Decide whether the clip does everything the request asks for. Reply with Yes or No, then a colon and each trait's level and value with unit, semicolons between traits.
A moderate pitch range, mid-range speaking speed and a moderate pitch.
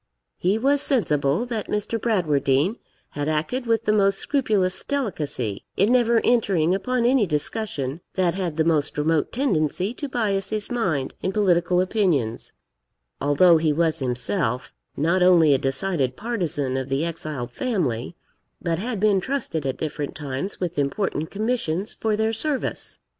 No: wide, 6.7 semitones; average, 150 wpm; medium, 180 Hz